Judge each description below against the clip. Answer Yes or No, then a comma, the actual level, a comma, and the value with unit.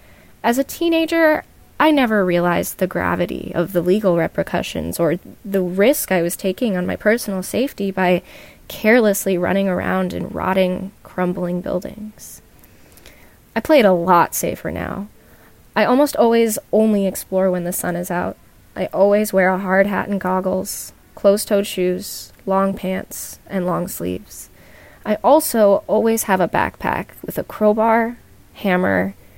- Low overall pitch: No, high, 195 Hz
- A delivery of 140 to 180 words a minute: Yes, average, 150 wpm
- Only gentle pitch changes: No, average, 3.0 semitones